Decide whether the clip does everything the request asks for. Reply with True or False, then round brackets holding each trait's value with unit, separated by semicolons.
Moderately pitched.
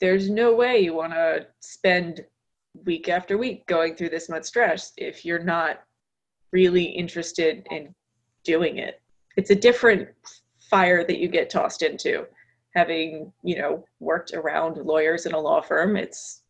True (175 Hz)